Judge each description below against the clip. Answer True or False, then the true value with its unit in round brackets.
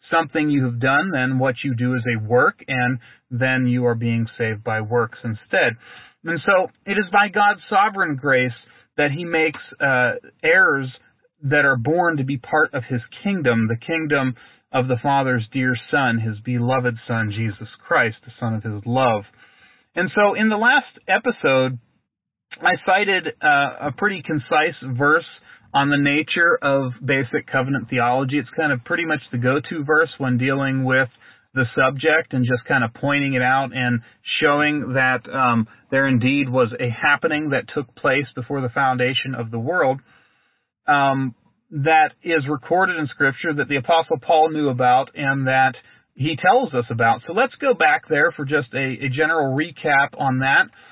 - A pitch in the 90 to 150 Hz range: True (135 Hz)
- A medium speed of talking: True (175 wpm)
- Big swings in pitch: False (3.9 semitones)